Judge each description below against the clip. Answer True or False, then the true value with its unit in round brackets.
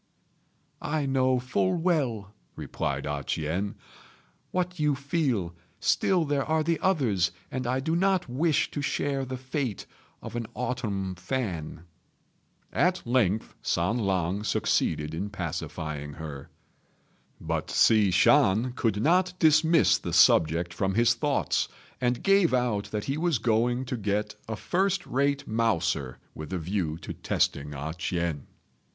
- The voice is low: True (115 Hz)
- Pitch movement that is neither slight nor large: False (7.6 semitones)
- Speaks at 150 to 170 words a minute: False (140 wpm)